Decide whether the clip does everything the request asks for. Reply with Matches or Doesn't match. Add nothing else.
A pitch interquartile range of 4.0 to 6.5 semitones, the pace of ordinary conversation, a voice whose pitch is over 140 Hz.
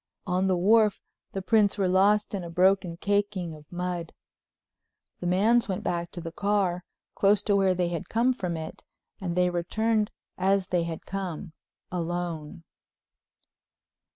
Doesn't match